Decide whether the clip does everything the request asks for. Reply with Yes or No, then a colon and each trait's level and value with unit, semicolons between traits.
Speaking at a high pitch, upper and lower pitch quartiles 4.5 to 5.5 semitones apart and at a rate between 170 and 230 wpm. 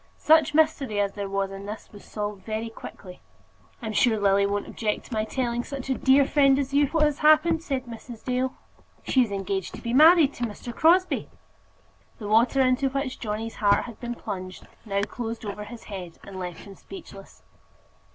Yes: high, 235 Hz; average, 5.2 semitones; average, 190 wpm